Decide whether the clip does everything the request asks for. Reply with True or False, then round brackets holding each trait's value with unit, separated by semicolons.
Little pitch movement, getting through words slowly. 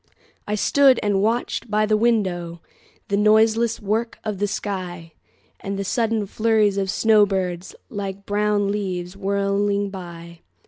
True (2.0 semitones; 125 wpm)